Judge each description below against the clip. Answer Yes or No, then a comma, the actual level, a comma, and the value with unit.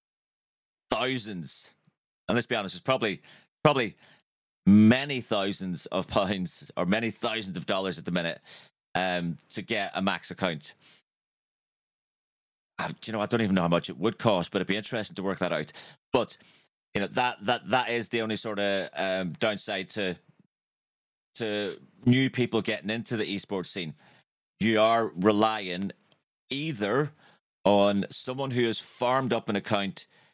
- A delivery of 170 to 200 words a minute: No, average, 160 wpm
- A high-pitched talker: No, low, 110 Hz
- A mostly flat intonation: No, average, 3.5 semitones